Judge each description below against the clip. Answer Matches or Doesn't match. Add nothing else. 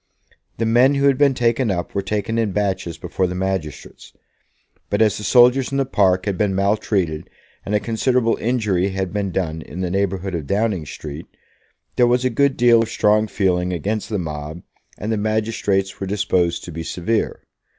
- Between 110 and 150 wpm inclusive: Doesn't match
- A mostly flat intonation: Doesn't match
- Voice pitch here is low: Matches